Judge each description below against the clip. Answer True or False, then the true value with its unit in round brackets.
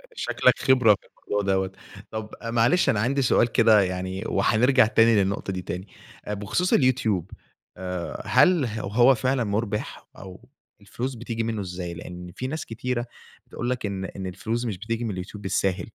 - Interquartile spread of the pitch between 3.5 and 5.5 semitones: True (3.9 semitones)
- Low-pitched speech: True (110 Hz)